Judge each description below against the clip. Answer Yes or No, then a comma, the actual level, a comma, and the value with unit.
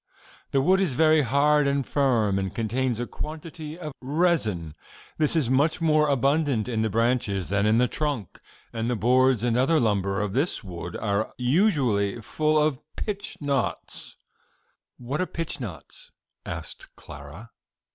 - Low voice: Yes, low, 130 Hz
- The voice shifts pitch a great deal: Yes, wide, 5.8 semitones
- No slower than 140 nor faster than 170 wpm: Yes, average, 155 wpm